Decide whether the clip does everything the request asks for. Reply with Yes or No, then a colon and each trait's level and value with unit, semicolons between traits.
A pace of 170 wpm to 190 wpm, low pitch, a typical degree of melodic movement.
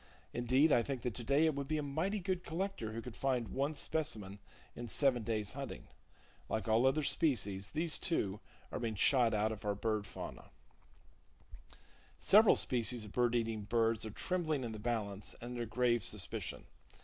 Yes: average, 175 wpm; low, 120 Hz; average, 4.7 semitones